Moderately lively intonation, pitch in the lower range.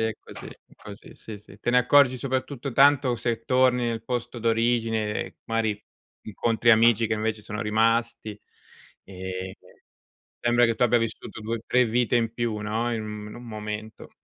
No: narrow, 1.9 semitones; low, 115 Hz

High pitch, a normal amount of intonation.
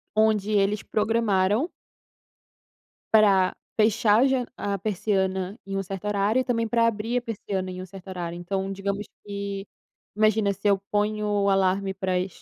No: high, 200 Hz; narrow, 2.0 semitones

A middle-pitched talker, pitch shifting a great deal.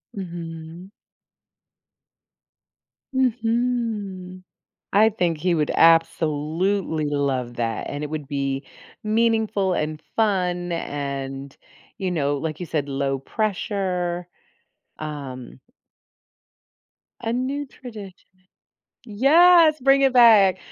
Yes: medium, 180 Hz; wide, 6.7 semitones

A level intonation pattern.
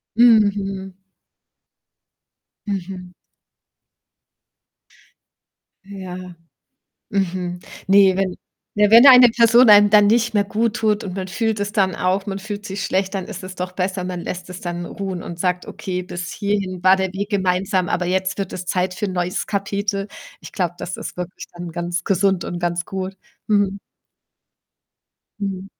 Yes: narrow, 1.9 semitones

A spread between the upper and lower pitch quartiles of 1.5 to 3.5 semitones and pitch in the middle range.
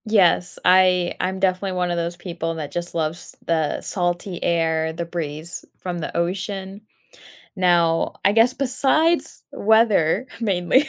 Yes: average, 2.8 semitones; medium, 180 Hz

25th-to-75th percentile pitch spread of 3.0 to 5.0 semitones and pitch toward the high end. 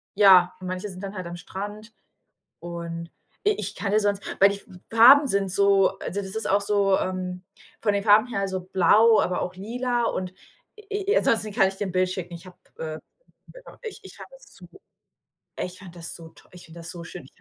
No: narrow, 2.6 semitones; high, 195 Hz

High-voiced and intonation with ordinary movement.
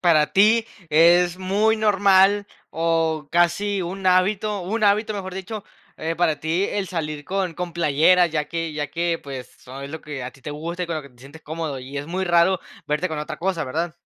No: medium, 170 Hz; average, 3.7 semitones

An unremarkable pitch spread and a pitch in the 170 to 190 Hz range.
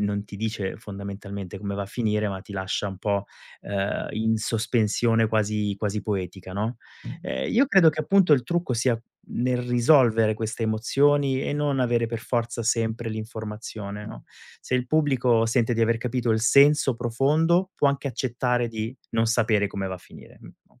No: average, 3.2 semitones; low, 115 Hz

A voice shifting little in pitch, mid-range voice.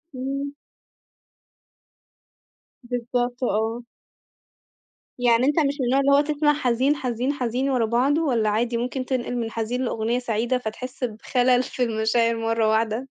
No: narrow, 2.3 semitones; high, 245 Hz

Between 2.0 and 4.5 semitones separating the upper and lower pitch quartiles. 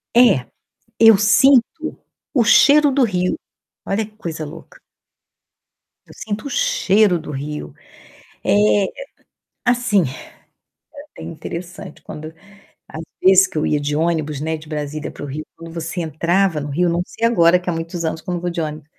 No: average, 5.3 semitones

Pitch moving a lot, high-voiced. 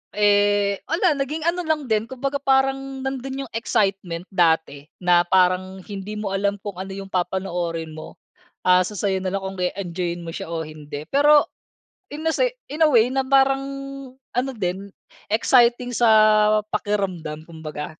Yes: wide, 7.0 semitones; high, 200 Hz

